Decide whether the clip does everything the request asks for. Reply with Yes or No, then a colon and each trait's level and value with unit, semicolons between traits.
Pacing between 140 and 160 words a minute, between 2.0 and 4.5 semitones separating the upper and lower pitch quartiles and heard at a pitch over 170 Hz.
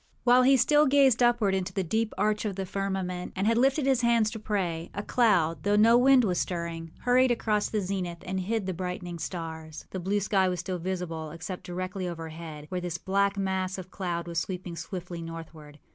No: fast, 205 wpm; average, 3.8 semitones; high, 190 Hz